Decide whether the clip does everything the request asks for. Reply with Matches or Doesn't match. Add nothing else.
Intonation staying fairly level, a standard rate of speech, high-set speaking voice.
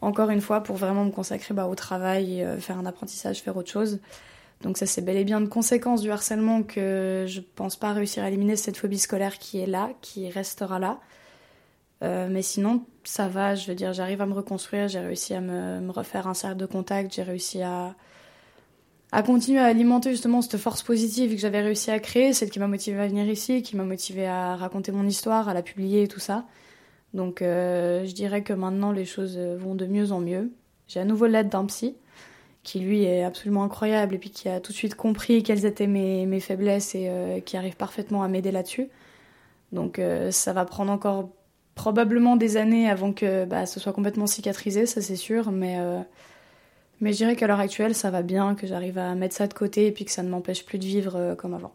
Doesn't match